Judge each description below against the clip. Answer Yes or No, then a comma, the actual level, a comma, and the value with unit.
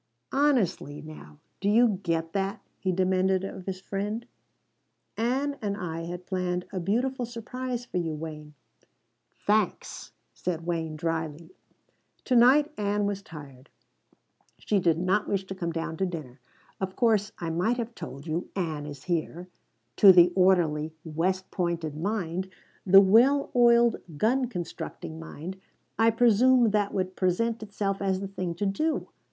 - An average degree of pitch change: Yes, average, 4.6 semitones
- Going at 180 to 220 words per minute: No, average, 150 wpm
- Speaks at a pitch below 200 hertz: Yes, high, 190 Hz